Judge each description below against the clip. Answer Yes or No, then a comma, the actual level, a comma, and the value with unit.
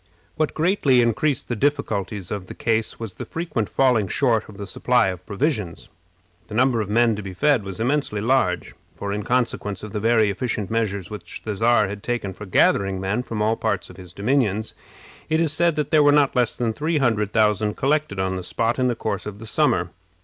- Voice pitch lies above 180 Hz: No, low, 110 Hz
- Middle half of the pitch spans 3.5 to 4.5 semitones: Yes, average, 4.2 semitones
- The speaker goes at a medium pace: No, fast, 215 wpm